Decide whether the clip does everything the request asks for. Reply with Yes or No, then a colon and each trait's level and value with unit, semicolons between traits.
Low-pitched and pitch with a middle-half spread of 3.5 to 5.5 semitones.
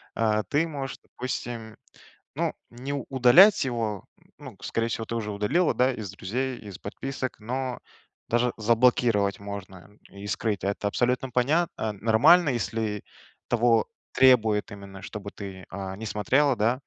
Yes: low, 115 Hz; average, 3.8 semitones